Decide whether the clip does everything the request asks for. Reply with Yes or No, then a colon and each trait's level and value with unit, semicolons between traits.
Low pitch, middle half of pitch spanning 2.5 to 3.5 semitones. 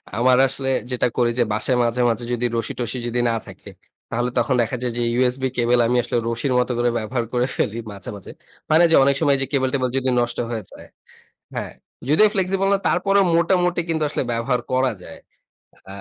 Yes: low, 125 Hz; average, 2.8 semitones